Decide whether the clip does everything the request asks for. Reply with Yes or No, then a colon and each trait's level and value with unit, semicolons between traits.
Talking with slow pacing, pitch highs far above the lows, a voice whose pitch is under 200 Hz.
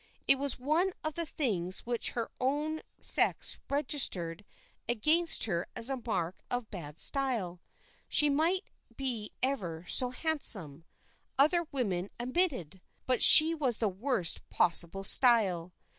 No: slow, 130 wpm; wide, 7.8 semitones; high, 245 Hz